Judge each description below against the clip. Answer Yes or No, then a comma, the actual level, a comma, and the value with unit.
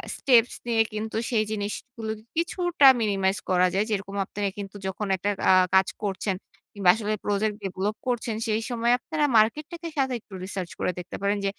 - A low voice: No, high, 215 Hz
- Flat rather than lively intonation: No, average, 3.2 semitones